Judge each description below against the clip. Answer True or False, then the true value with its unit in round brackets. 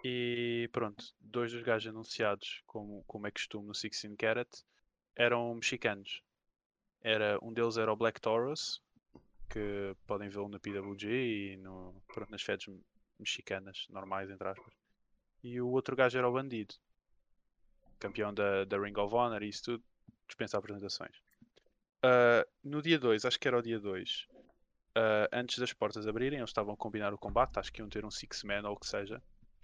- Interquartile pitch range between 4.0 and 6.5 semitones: False (2.8 semitones)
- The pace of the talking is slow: False (175 wpm)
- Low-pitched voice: True (110 Hz)